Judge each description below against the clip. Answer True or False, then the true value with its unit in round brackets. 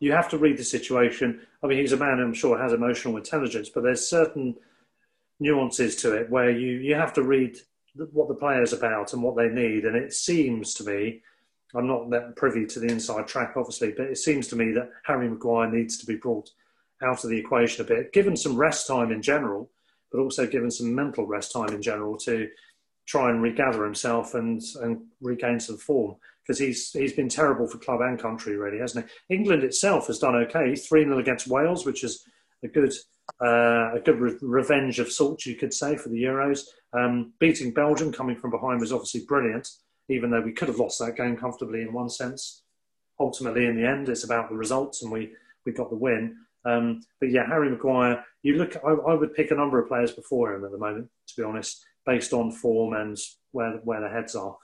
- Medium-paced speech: False (220 wpm)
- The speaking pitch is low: True (125 Hz)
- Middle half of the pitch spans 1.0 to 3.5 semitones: True (3.0 semitones)